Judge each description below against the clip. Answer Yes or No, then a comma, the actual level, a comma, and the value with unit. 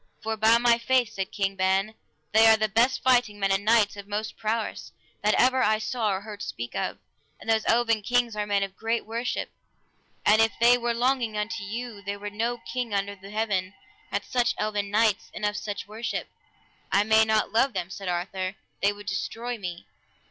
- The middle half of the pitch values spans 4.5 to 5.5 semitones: No, narrow, 2.4 semitones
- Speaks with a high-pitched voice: Yes, high, 215 Hz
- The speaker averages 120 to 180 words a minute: No, average, 200 wpm